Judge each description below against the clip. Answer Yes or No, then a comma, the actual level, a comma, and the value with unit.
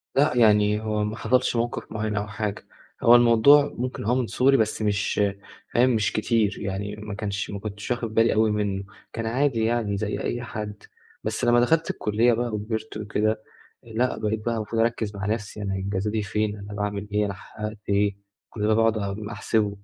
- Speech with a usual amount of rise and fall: No, narrow, 2.0 semitones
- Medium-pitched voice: No, low, 110 Hz